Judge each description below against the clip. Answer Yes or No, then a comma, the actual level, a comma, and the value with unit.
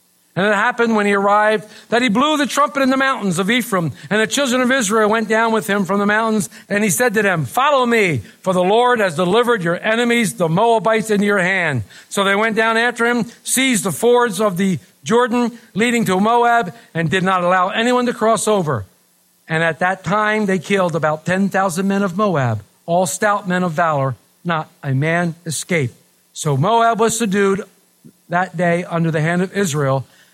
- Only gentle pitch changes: No, average, 4.4 semitones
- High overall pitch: Yes, high, 200 Hz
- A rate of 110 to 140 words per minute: No, average, 200 wpm